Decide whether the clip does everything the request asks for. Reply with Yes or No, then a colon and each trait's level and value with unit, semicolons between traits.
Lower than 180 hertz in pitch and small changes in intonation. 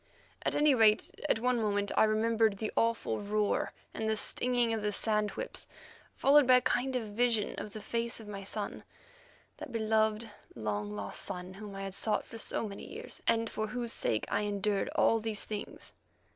No: high, 215 Hz; narrow, 2.1 semitones